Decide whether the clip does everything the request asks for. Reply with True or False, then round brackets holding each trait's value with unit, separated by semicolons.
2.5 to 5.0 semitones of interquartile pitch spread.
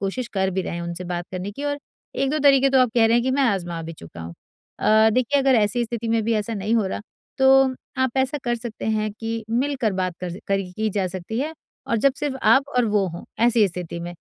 False (5.4 semitones)